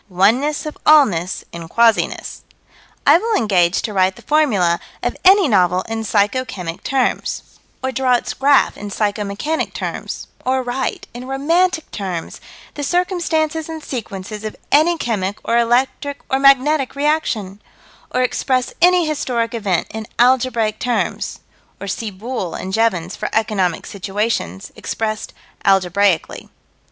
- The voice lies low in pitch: No, high, 230 Hz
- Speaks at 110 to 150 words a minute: Yes, average, 140 wpm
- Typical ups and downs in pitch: No, wide, 6.0 semitones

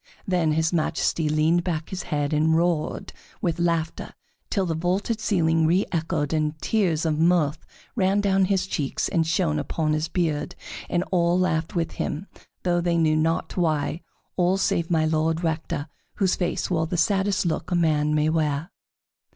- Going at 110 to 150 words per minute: No, average, 165 wpm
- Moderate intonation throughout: No, narrow, 2.3 semitones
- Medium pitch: Yes, medium, 165 Hz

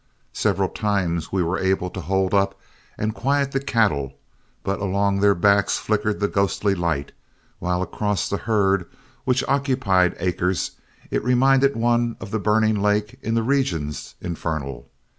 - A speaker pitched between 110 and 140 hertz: No, low, 100 Hz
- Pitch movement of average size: Yes, average, 3.8 semitones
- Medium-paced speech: Yes, average, 150 wpm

